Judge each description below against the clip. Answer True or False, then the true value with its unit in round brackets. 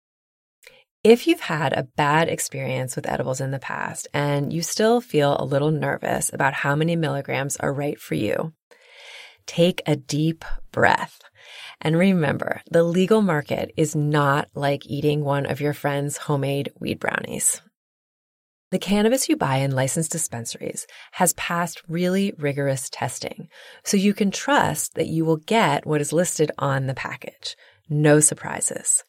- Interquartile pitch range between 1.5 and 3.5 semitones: False (4.4 semitones)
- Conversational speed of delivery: True (155 wpm)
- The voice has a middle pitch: True (155 Hz)